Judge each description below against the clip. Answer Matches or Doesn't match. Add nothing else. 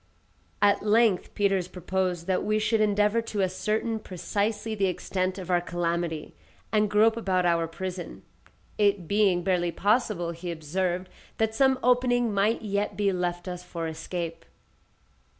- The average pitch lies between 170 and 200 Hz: Matches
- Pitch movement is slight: Doesn't match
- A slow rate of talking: Doesn't match